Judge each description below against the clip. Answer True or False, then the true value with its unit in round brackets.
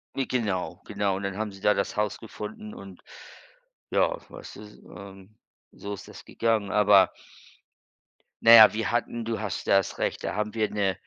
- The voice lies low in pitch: True (105 Hz)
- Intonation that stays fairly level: True (1.9 semitones)